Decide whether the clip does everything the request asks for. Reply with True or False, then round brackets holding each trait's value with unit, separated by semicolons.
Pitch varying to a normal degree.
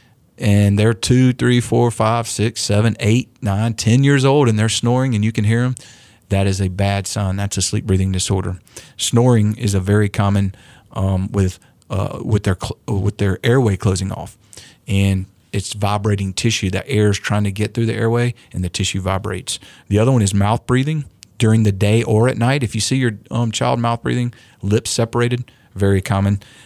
True (3.3 semitones)